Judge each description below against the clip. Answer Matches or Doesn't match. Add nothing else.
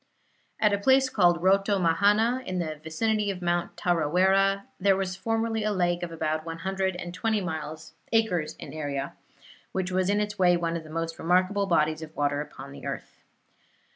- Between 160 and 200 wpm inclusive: Matches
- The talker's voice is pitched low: Doesn't match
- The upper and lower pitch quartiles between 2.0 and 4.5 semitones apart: Matches